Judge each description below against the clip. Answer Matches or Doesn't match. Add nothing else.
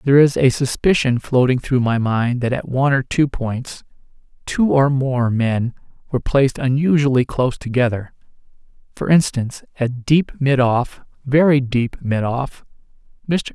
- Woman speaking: Doesn't match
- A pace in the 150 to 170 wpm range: Doesn't match